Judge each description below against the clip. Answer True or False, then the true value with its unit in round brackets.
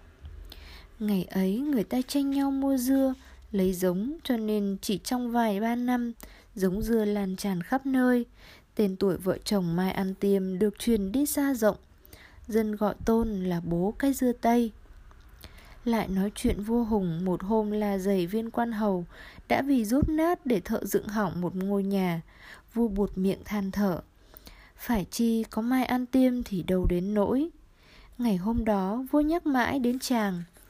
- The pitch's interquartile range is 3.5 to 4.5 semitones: True (4.1 semitones)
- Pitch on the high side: True (215 Hz)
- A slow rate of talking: False (175 wpm)